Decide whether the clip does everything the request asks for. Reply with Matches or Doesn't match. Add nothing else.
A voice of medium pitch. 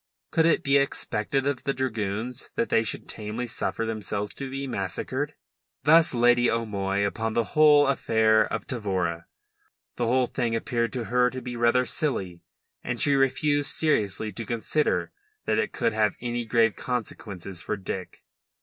Doesn't match